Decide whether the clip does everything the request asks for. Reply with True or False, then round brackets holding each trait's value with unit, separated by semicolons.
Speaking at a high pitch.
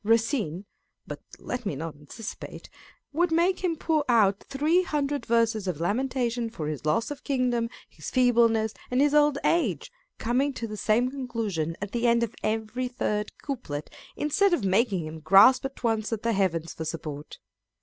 True (230 Hz)